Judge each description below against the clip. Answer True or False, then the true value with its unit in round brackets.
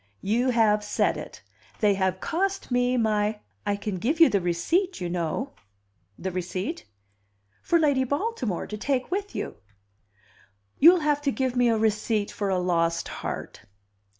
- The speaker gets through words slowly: False (160 wpm)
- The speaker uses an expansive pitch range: True (6.8 semitones)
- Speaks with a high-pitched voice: True (220 Hz)